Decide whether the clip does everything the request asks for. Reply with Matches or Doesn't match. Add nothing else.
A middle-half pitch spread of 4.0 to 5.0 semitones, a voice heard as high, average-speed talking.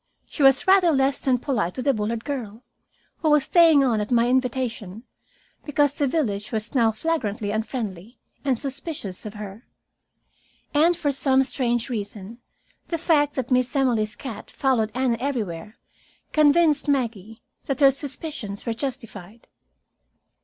Matches